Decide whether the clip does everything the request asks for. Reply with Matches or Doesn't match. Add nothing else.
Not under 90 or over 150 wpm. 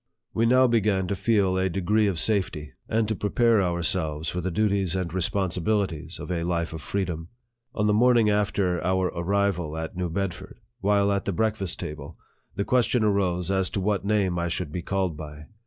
Doesn't match